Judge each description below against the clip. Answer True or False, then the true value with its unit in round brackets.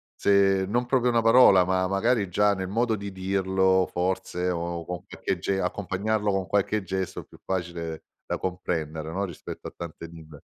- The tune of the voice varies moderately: False (2.3 semitones)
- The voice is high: False (95 Hz)